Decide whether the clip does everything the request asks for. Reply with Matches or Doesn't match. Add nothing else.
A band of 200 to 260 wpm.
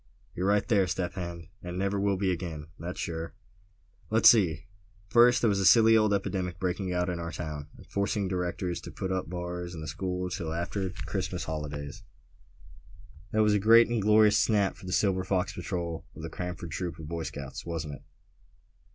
Matches